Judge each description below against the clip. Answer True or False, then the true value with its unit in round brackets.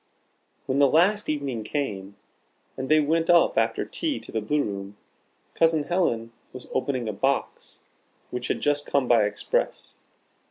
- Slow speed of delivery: False (155 wpm)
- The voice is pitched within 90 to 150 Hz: True (140 Hz)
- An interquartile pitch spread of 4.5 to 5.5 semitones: True (5.2 semitones)